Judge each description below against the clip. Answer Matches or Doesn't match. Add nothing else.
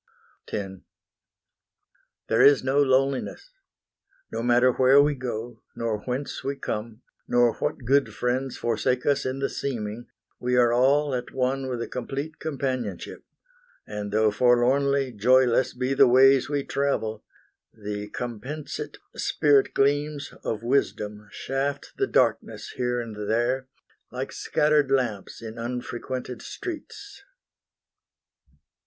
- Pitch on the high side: Doesn't match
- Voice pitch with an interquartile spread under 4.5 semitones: Matches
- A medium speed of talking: Doesn't match